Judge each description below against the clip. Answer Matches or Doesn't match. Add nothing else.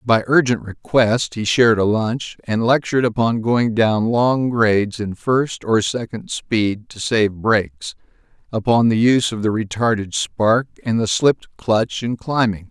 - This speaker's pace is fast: Doesn't match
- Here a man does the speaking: Matches